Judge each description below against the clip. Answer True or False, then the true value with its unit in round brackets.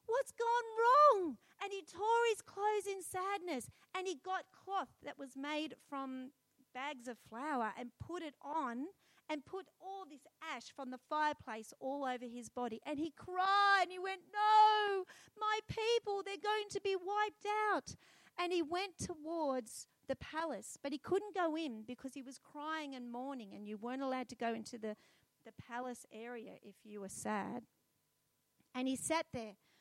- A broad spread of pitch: True (7.2 semitones)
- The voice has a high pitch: True (310 Hz)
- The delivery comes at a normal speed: True (175 wpm)